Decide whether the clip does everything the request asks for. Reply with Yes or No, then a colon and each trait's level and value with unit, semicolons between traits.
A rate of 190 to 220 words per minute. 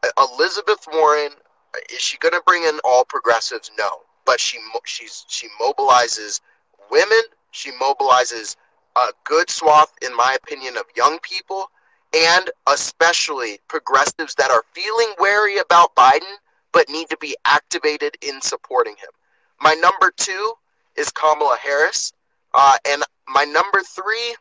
No: average, 140 wpm